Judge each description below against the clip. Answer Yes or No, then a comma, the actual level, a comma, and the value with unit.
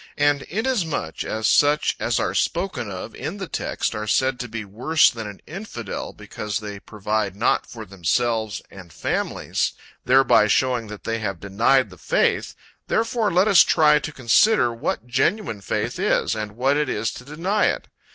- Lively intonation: Yes, wide, 6.1 semitones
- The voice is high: No, low, 120 Hz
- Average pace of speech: Yes, average, 170 wpm